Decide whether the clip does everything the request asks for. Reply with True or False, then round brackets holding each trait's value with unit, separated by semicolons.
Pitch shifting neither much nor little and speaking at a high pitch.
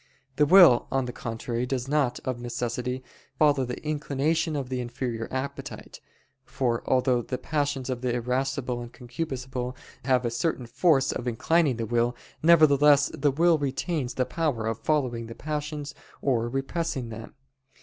False (3.3 semitones; 130 Hz)